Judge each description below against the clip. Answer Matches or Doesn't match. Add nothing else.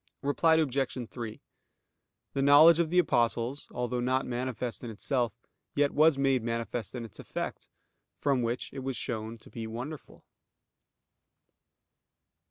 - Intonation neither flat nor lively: Matches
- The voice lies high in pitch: Doesn't match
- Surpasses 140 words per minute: Doesn't match